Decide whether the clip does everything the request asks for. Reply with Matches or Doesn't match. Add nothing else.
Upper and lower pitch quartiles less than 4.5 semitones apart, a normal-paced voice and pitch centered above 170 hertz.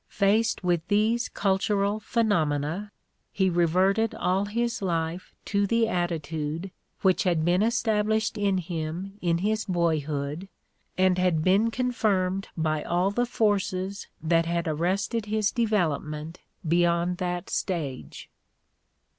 Doesn't match